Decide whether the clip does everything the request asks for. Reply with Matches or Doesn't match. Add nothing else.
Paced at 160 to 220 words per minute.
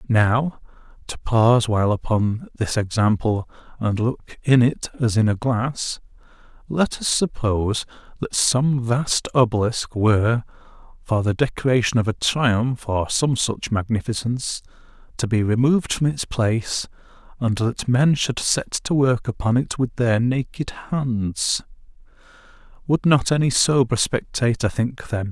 Doesn't match